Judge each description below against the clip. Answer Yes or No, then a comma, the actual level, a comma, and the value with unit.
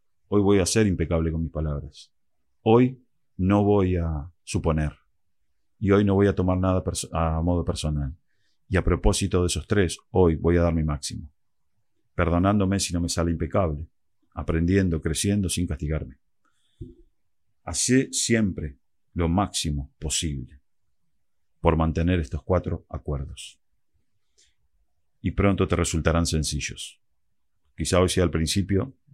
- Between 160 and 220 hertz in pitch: No, very low, 85 Hz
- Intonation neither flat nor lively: Yes, average, 3.6 semitones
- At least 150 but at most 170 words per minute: No, average, 135 wpm